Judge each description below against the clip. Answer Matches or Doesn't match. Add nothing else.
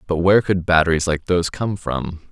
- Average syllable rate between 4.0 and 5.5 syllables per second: Doesn't match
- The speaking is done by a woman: Doesn't match